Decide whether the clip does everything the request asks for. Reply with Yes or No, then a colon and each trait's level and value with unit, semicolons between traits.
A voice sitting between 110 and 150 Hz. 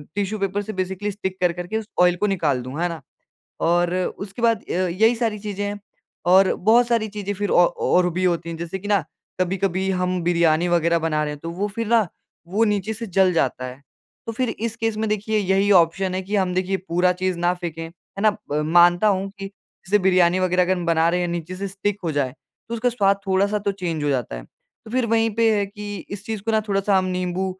No: high, 190 Hz